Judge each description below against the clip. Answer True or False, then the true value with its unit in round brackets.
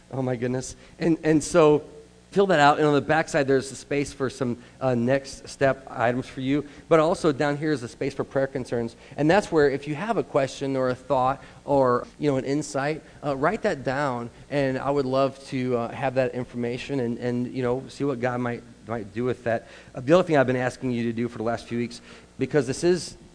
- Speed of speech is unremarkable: False (240 wpm)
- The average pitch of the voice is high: False (135 Hz)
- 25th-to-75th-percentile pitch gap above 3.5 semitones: False (2.8 semitones)